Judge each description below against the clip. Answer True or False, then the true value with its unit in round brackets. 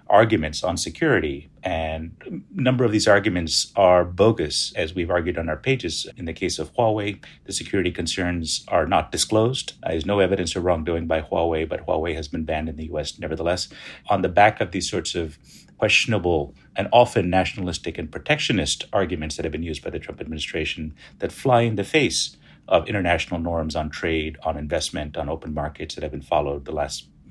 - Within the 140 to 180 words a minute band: False (190 wpm)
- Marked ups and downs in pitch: False (3.6 semitones)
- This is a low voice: True (85 Hz)